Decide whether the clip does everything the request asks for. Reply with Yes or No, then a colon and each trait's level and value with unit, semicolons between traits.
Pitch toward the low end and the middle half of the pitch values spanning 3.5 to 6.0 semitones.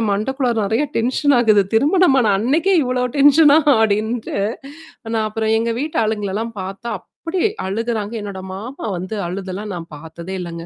No: high, 220 Hz; average, 4.7 semitones